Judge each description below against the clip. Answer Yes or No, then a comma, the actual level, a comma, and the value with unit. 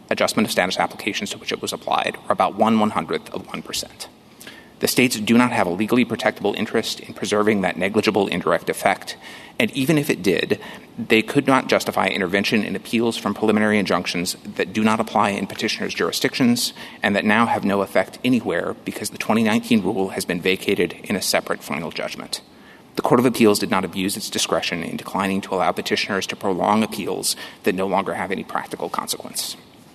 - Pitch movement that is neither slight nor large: No, wide, 5.7 semitones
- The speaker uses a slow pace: No, average, 190 wpm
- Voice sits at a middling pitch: No, low, 110 Hz